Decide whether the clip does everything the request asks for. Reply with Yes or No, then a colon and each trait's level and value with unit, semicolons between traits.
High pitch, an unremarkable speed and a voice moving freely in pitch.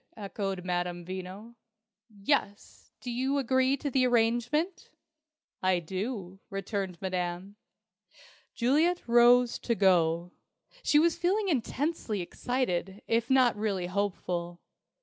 No: high, 210 Hz; slow, 110 wpm; wide, 5.8 semitones